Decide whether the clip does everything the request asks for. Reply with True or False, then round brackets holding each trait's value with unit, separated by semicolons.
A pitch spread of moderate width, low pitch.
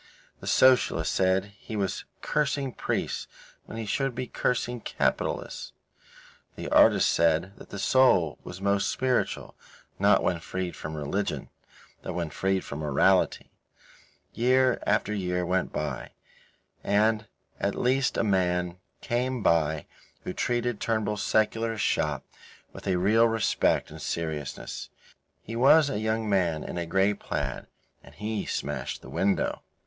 True (4.5 semitones; 100 Hz)